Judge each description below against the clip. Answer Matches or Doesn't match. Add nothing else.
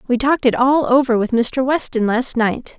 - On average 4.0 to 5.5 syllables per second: Matches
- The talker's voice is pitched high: Matches